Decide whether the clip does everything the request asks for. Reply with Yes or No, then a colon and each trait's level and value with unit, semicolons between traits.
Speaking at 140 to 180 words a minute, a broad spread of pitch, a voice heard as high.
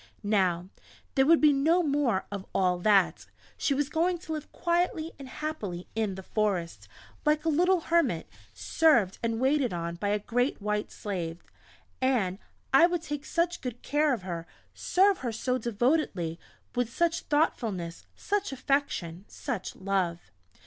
Yes: average, 155 wpm; wide, 8.3 semitones; high, 245 Hz